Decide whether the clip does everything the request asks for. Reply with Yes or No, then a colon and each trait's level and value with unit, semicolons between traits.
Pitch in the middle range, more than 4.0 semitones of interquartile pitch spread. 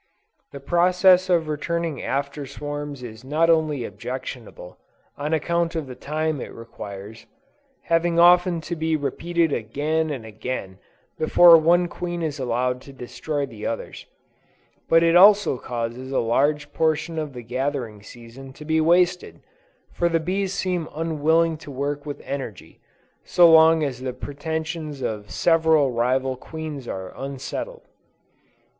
Yes: medium, 150 Hz; average, 4.4 semitones